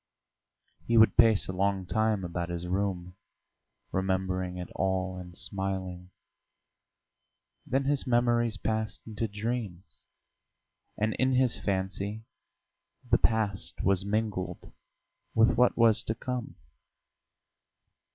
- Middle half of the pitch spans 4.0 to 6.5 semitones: No, average, 3.3 semitones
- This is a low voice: Yes, low, 100 Hz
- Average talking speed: No, slow, 110 wpm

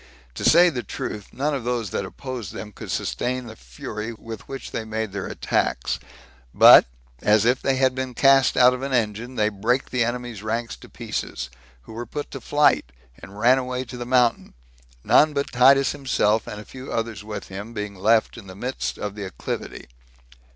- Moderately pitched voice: No, low, 120 Hz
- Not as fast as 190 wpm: No, average, 195 wpm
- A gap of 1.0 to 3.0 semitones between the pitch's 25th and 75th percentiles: No, average, 3.5 semitones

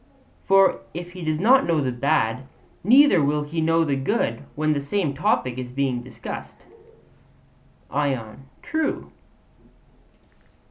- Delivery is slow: Yes, slow, 130 wpm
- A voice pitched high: No, medium, 150 Hz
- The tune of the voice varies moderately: Yes, average, 5.0 semitones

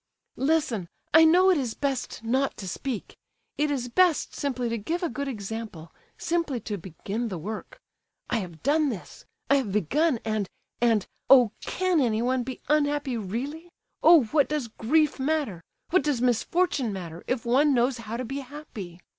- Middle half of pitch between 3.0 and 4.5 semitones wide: No, average, 5.2 semitones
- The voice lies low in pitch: No, very high, 255 Hz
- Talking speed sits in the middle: Yes, average, 150 wpm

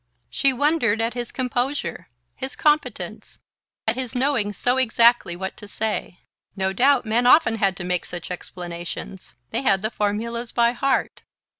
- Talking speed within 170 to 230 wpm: No, average, 155 wpm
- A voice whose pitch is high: Yes, high, 230 Hz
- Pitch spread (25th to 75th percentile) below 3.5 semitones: No, average, 4.7 semitones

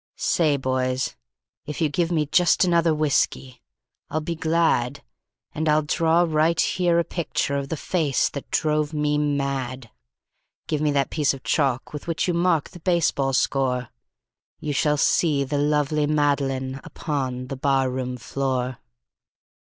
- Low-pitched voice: No, medium, 150 Hz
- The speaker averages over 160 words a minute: No, average, 150 wpm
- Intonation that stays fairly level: No, average, 3.0 semitones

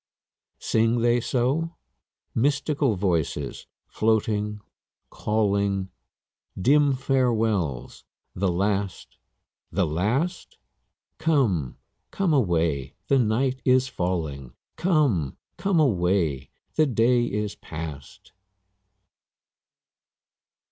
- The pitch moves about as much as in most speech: No, wide, 6.9 semitones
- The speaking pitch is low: Yes, low, 110 Hz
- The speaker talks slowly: Yes, slow, 80 wpm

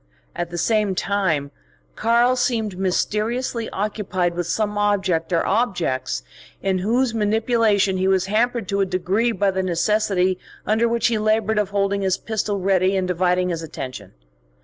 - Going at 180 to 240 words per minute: No, average, 155 wpm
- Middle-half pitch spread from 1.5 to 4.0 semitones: Yes, average, 3.0 semitones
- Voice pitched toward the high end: Yes, high, 200 Hz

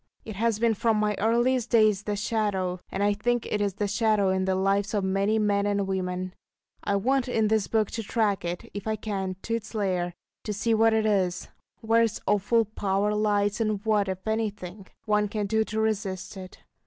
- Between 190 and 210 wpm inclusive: Yes, fast, 205 wpm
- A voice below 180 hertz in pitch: No, high, 210 Hz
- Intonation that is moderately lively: No, narrow, 2.1 semitones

